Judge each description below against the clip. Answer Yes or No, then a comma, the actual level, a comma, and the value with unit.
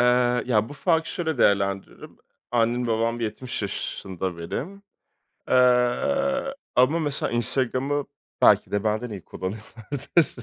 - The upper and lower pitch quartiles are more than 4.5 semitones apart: Yes, average, 5.2 semitones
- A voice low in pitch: Yes, low, 125 Hz